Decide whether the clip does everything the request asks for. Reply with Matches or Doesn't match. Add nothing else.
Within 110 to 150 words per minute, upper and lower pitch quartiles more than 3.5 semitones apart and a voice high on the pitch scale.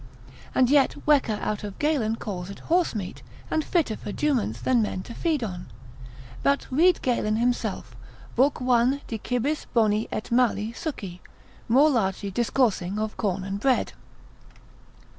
Matches